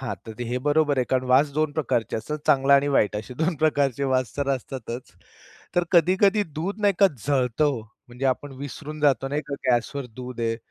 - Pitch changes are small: No, average, 3.4 semitones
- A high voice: No, medium, 140 Hz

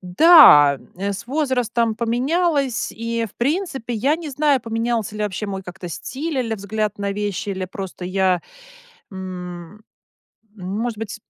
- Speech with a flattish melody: No, average, 4.8 semitones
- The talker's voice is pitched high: Yes, high, 220 Hz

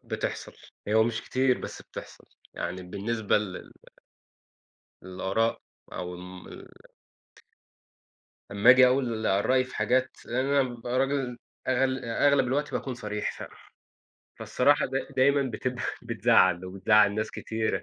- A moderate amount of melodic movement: Yes, average, 3.9 semitones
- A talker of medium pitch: No, low, 120 Hz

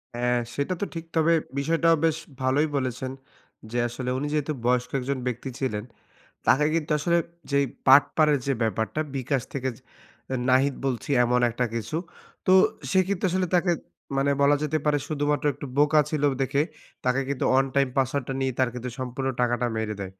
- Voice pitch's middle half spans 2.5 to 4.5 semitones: Yes, average, 3.0 semitones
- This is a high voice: No, low, 135 Hz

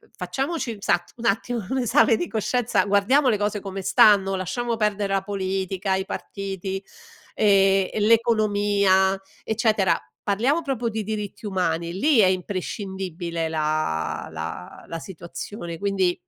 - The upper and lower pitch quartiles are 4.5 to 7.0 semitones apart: No, average, 2.7 semitones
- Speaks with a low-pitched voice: No, high, 195 Hz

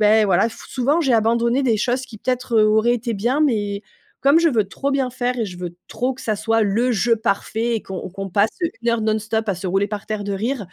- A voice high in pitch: Yes, high, 225 Hz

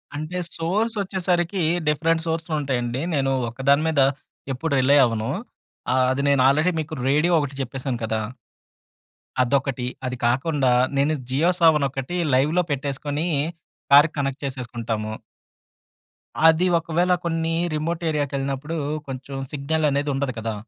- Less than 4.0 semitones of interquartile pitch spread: Yes, average, 3.6 semitones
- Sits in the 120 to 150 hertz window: Yes, medium, 140 Hz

